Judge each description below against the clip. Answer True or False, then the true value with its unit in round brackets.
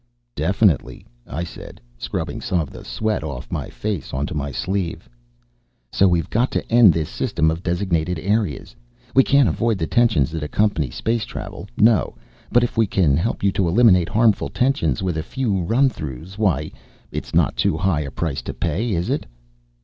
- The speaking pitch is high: False (90 Hz)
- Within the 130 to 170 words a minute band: False (180 wpm)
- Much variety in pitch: True (5.8 semitones)